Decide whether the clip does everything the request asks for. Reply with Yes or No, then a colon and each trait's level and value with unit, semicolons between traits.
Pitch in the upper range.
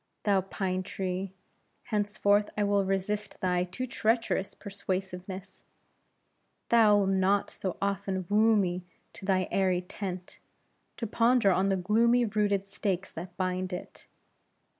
Yes: high, 195 Hz